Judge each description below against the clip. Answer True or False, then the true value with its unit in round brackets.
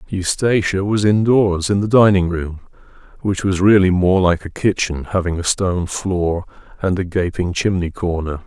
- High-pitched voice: False (95 Hz)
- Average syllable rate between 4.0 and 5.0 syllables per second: True (4.7 syllables/s)